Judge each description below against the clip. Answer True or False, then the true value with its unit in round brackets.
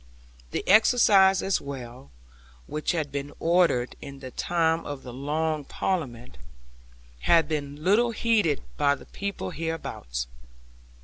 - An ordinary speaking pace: False (125 wpm)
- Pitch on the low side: False (155 Hz)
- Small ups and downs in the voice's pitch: False (4.8 semitones)